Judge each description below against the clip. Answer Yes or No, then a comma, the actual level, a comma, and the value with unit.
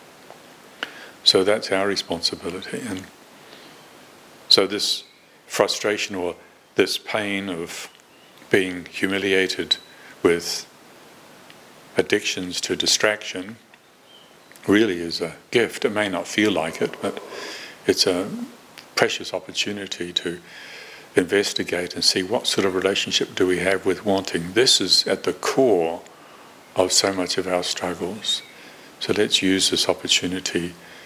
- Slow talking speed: Yes, slow, 120 wpm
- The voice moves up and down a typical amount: No, narrow, 1.7 semitones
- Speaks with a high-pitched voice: No, very low, 95 Hz